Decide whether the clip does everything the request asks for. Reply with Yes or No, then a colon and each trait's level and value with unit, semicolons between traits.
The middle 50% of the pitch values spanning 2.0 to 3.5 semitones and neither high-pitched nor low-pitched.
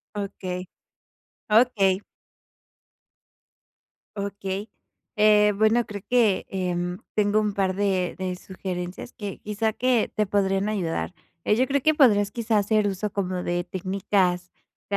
No: narrow, 2.4 semitones; high, 200 Hz